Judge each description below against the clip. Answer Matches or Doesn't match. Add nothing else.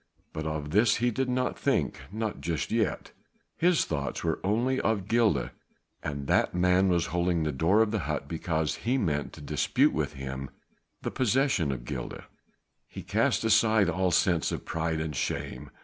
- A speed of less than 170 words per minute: Doesn't match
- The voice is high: Doesn't match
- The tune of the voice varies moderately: Doesn't match